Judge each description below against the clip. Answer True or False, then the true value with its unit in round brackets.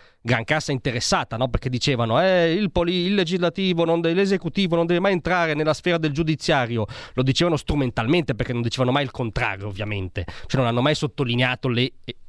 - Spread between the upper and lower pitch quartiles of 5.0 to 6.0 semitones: True (5.6 semitones)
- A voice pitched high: False (140 Hz)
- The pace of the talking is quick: True (185 wpm)